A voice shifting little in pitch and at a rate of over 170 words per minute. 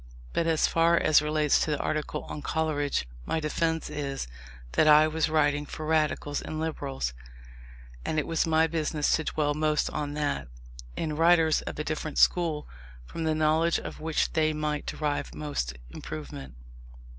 No: narrow, 1.4 semitones; average, 165 wpm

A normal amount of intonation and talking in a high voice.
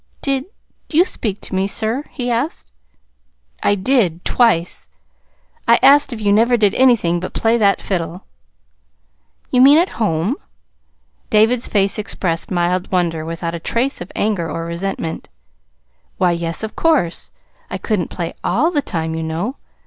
No: wide, 6.1 semitones; high, 200 Hz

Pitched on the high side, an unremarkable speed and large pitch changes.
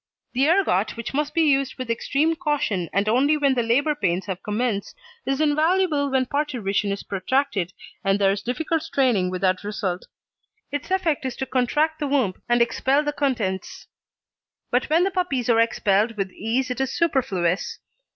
Yes: very high, 255 Hz; average, 170 wpm; wide, 6.4 semitones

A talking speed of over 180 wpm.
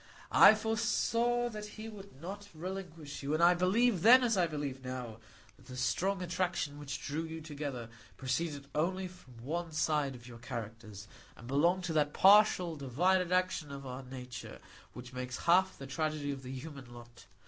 No: average, 175 wpm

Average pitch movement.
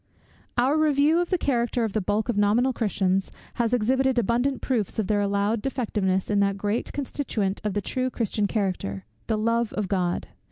Yes: average, 4.0 semitones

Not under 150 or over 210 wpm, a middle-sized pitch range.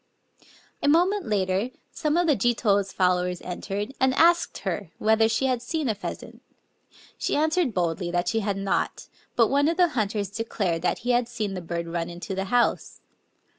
No: average, 180 wpm; wide, 5.8 semitones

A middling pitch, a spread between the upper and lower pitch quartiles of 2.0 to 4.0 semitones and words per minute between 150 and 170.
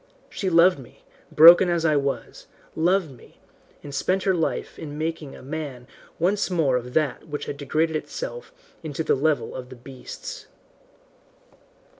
Yes: medium, 155 Hz; average, 3.6 semitones; average, 155 wpm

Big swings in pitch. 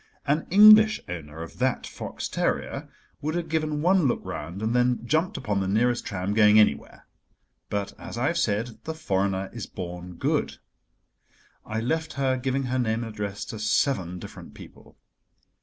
Yes: wide, 6.8 semitones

